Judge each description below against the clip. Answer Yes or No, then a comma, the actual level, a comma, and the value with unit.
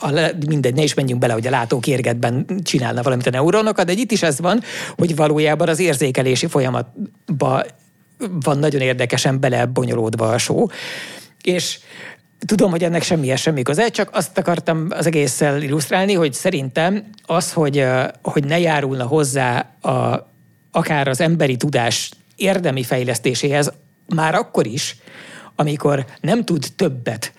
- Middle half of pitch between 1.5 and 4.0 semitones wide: No, average, 4.5 semitones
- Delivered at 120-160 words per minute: Yes, average, 145 wpm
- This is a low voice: No, medium, 150 Hz